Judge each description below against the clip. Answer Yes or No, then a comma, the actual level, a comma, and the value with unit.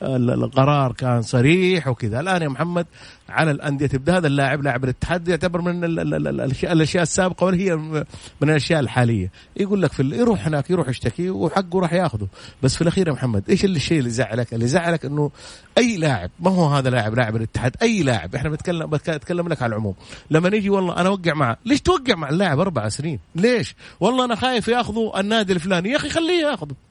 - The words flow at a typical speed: No, fast, 190 wpm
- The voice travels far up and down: Yes, wide, 6.0 semitones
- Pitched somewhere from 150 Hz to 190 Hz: Yes, medium, 160 Hz